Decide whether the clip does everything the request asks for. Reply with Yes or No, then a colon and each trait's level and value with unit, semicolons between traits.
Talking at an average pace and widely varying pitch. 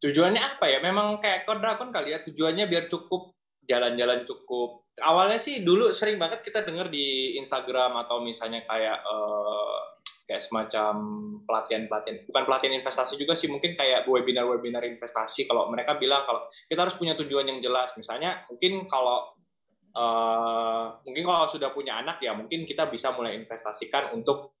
No: fast, 160 wpm; wide, 6.6 semitones